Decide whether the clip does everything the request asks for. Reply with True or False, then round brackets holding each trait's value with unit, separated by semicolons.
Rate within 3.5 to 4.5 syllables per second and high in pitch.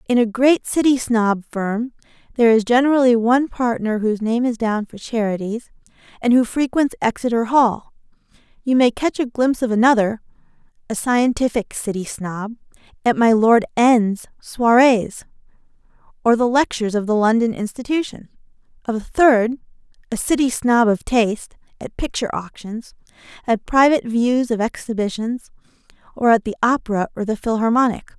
False (4.8 syllables/s; 235 Hz)